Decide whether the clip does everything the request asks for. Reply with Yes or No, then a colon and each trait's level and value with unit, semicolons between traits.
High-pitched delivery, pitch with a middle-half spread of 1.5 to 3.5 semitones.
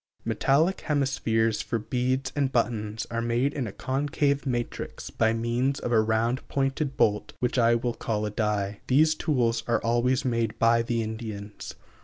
No: low, 120 Hz; average, 3.0 semitones